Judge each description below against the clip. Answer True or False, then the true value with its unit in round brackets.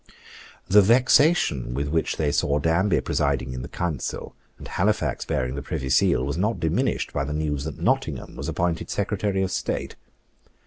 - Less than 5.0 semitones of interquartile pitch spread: False (5.4 semitones)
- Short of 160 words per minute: False (170 wpm)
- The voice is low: True (80 Hz)